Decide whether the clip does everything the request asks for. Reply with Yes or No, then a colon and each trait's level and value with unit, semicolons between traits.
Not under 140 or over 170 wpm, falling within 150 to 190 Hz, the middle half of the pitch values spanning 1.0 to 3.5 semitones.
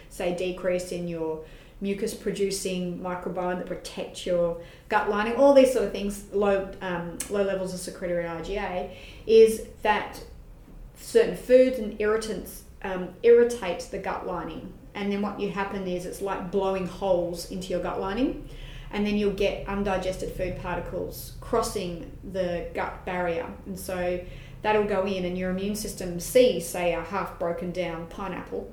Yes: average, 160 wpm; medium, 185 Hz; narrow, 2.4 semitones